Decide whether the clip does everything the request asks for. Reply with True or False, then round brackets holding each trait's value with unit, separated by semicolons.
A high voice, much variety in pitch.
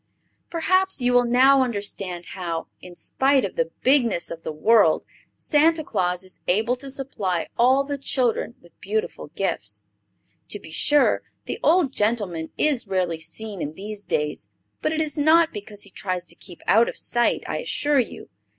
True (220 Hz; 7.2 semitones)